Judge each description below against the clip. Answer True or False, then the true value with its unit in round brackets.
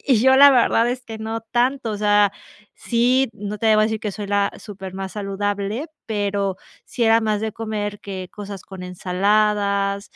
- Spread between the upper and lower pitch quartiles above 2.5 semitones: False (2.1 semitones)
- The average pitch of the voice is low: False (210 Hz)